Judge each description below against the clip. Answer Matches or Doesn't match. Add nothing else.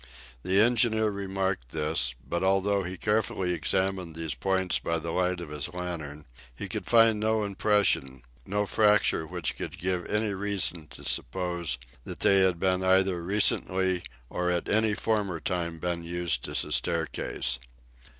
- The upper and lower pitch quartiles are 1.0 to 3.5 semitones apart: Matches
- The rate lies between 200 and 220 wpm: Doesn't match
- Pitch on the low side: Matches